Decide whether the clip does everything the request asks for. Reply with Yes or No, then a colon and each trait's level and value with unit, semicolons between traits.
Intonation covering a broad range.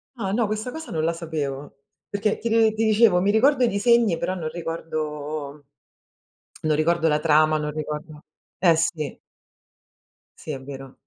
Yes: wide, 5.8 semitones